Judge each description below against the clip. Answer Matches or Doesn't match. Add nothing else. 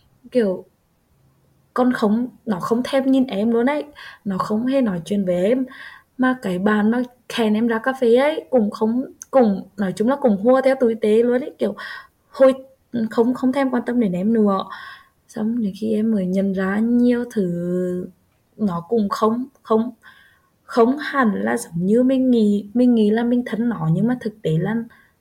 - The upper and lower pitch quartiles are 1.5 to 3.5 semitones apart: Matches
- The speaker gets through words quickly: Doesn't match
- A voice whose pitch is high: Matches